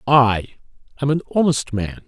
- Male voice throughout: Yes, male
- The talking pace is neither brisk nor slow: Yes, average, 145 wpm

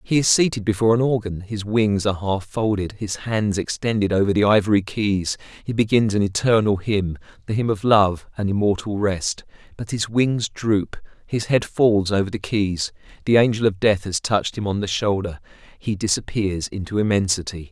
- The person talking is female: No, male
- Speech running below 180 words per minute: No, average, 185 wpm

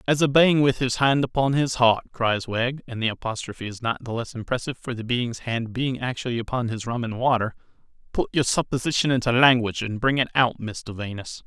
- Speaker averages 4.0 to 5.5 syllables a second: No, 5.7 syllables/s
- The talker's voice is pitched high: No, low, 120 Hz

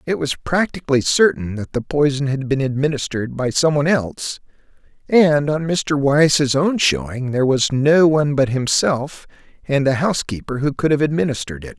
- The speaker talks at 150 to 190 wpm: Yes, average, 170 wpm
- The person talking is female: No, male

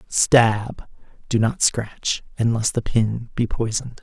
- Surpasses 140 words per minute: No, slow, 135 wpm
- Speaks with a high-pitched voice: No, low, 115 Hz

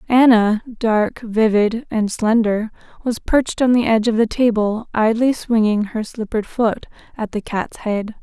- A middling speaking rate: Yes, average, 160 wpm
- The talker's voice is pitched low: No, high, 225 Hz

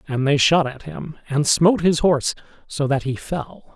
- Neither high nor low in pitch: Yes, medium, 150 Hz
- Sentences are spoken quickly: Yes, fast, 210 wpm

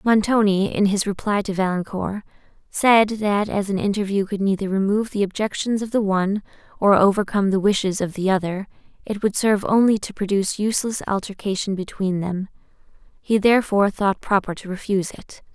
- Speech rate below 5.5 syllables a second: No, 5.7 syllables/s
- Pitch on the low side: No, high, 200 Hz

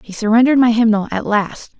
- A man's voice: No, female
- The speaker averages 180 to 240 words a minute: Yes, average, 200 wpm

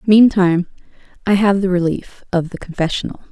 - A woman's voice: Yes, female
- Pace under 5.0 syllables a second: No, 5.5 syllables/s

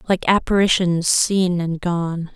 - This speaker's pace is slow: Yes, slow, 125 wpm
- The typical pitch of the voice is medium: Yes, medium, 180 Hz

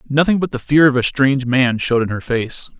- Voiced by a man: Yes, male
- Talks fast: Yes, fast, 260 wpm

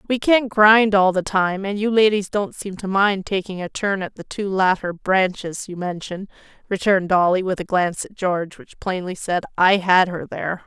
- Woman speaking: Yes, female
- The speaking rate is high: Yes, fast, 210 wpm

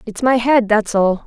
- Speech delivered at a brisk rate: Yes, fast, 235 wpm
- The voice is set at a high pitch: Yes, high, 225 Hz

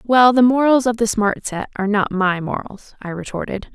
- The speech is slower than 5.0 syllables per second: No, 5.1 syllables/s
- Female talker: Yes, female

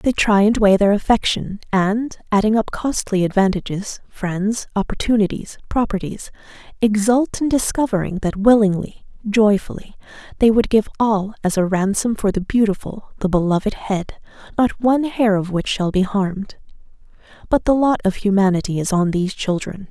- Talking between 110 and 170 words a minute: Yes, average, 150 wpm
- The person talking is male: No, female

